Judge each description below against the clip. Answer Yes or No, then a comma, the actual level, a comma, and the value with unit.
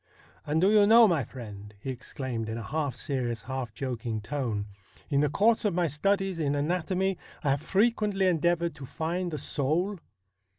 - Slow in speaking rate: No, average, 185 wpm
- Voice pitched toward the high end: No, medium, 150 Hz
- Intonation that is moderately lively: No, wide, 6.2 semitones